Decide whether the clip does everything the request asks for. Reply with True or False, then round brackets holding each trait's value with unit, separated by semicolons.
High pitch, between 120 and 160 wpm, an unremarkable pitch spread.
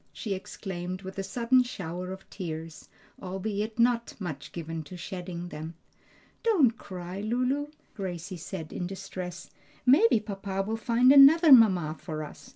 True (195 Hz; 145 wpm; 4.9 semitones)